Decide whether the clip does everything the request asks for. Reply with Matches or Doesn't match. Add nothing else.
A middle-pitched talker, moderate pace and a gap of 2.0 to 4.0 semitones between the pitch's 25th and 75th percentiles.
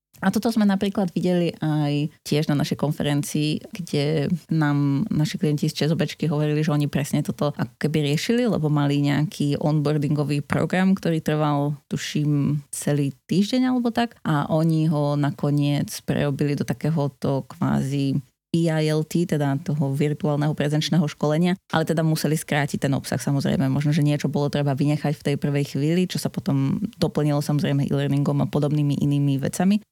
Matches